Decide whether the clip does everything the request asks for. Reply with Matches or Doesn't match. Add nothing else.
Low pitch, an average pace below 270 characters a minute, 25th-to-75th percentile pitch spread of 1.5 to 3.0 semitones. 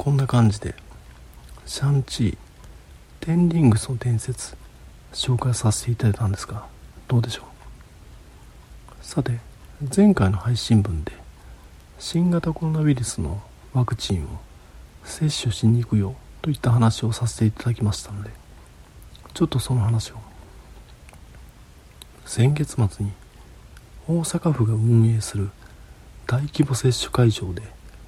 Doesn't match